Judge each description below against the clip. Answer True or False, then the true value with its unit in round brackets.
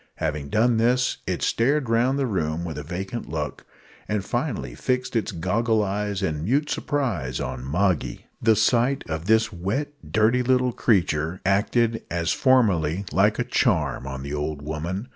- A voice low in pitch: True (100 Hz)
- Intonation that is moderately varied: False (6.9 semitones)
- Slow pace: False (160 wpm)